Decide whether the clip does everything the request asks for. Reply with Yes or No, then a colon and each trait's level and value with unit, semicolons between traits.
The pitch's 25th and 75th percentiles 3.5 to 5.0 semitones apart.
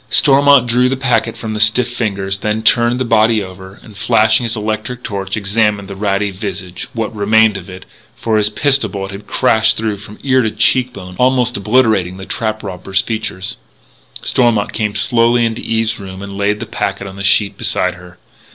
No: average, 2.8 semitones